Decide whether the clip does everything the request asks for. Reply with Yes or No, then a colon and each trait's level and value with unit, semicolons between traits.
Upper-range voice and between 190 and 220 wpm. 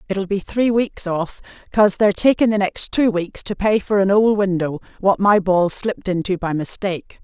Yes: high, 195 Hz; fast, 205 wpm